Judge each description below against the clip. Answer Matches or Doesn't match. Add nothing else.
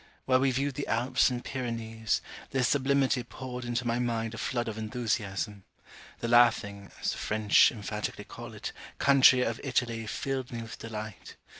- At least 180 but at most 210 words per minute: Doesn't match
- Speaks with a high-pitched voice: Doesn't match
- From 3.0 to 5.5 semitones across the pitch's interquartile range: Doesn't match